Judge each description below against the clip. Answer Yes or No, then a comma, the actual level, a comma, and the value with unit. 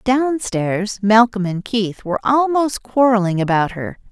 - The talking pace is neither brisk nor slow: Yes, average, 145 wpm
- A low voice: No, high, 220 Hz